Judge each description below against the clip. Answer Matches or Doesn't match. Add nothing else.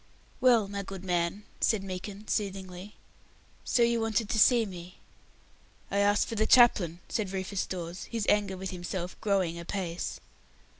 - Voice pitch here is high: Matches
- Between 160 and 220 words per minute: Doesn't match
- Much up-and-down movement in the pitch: Doesn't match